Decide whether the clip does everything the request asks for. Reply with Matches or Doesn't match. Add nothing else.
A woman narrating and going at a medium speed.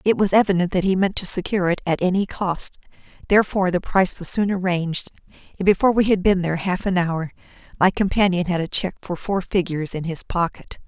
Doesn't match